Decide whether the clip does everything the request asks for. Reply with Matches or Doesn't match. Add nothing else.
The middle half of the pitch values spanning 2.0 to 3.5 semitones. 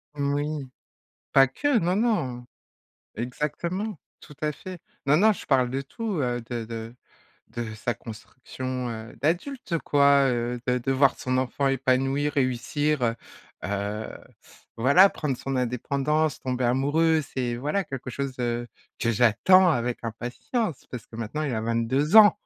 Doesn't match